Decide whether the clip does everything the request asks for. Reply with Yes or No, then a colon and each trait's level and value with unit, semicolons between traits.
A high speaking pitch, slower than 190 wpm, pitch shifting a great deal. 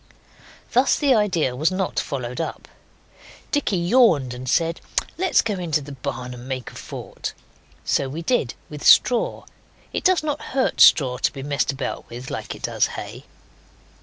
No: medium, 155 Hz; average, 165 wpm; wide, 8.8 semitones